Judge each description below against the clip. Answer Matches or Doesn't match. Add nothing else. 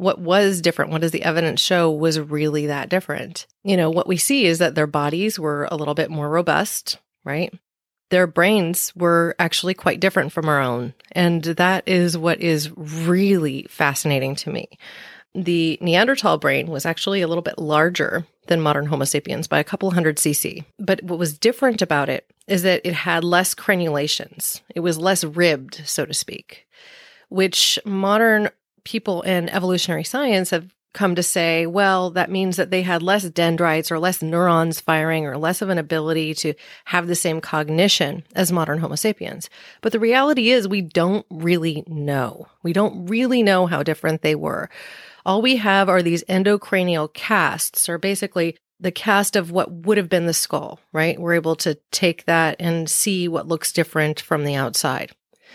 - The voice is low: Doesn't match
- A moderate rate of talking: Matches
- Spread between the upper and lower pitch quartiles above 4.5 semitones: Doesn't match